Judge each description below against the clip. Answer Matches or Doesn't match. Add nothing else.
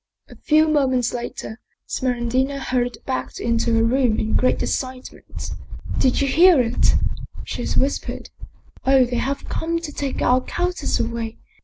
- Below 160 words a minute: Doesn't match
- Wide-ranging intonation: Doesn't match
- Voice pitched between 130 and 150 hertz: Doesn't match